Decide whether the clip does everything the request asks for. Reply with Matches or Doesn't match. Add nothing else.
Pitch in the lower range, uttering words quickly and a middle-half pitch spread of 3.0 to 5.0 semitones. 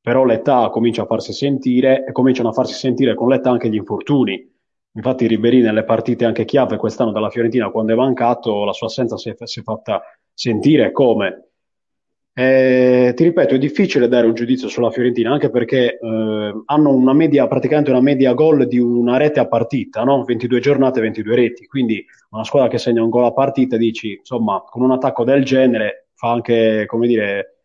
Doesn't match